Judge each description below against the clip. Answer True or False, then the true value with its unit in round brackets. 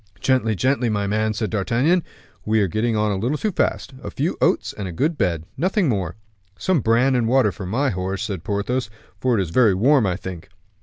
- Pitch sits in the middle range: False (110 Hz)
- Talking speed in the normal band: False (215 wpm)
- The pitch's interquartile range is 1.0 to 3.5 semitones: False (4.9 semitones)